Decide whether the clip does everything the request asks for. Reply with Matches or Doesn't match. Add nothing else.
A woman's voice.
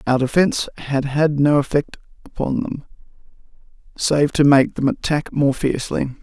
Doesn't match